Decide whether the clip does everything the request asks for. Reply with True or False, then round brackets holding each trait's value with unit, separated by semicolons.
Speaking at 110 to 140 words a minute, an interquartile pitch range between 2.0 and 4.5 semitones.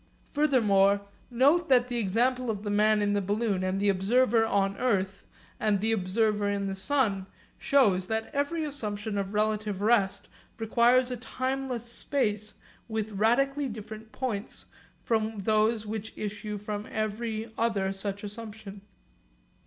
True (135 wpm; 2.8 semitones)